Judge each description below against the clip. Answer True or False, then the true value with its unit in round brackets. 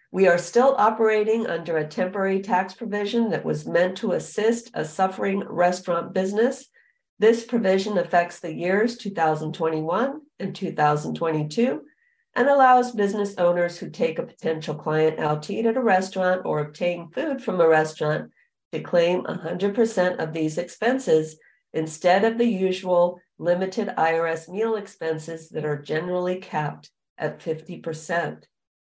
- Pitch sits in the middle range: True (180 Hz)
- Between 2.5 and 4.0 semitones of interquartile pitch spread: False (5.0 semitones)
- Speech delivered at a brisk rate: False (140 wpm)